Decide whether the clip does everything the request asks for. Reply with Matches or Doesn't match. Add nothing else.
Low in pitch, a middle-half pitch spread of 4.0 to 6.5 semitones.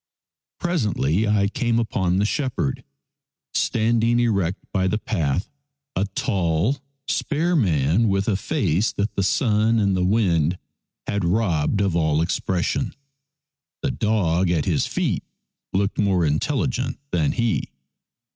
Matches